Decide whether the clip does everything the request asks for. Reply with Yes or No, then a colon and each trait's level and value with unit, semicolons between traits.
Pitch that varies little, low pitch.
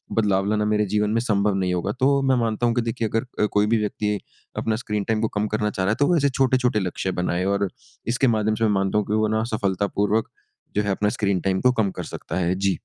Yes: narrow, 2.3 semitones; low, 105 Hz